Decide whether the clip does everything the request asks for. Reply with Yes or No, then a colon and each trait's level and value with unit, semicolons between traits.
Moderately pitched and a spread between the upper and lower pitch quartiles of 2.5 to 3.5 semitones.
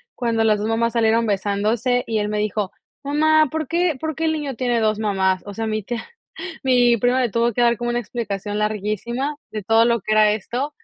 No: high, 230 Hz; average, 2.8 semitones